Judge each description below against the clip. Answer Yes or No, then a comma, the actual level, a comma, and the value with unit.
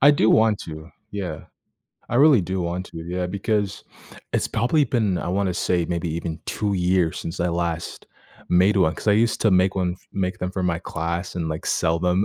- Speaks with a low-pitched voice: Yes, very low, 90 Hz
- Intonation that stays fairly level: No, average, 3.0 semitones